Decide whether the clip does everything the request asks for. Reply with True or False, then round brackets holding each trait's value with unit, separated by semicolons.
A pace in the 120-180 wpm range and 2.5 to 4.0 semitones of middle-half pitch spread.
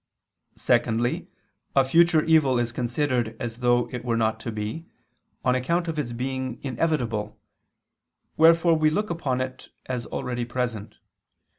False (140 wpm; 4.5 semitones)